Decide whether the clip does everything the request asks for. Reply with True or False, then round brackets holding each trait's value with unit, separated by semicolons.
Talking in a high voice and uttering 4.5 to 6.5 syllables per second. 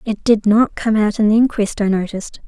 True (215 Hz; 5.6 syllables/s)